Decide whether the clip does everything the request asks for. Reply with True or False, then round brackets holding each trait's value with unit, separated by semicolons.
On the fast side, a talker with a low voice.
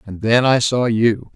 True (220 wpm; 115 Hz)